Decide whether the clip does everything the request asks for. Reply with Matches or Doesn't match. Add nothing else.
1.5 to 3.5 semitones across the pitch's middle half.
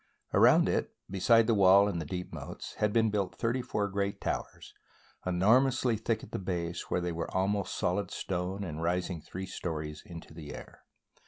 Matches